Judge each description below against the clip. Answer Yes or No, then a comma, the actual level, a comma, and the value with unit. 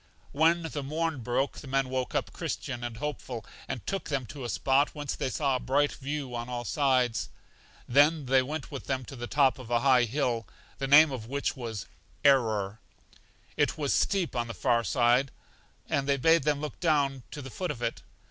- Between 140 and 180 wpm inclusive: No, fast, 205 wpm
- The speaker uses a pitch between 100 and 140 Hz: Yes, low, 135 Hz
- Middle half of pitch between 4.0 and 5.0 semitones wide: No, average, 3.1 semitones